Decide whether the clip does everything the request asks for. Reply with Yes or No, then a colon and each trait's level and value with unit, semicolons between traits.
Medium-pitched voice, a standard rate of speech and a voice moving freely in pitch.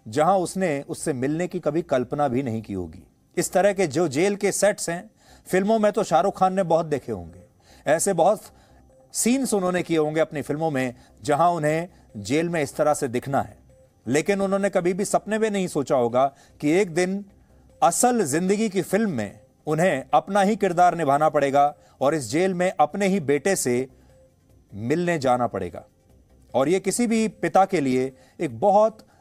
Yes: medium, 165 Hz; average, 185 wpm; wide, 5.9 semitones